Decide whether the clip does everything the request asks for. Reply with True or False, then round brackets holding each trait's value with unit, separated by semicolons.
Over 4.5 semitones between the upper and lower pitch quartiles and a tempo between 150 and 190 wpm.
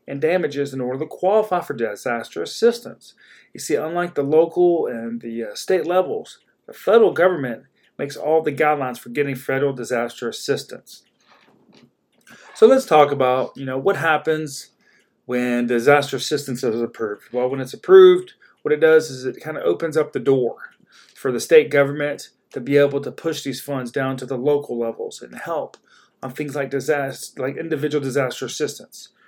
True (4.9 semitones; 175 wpm)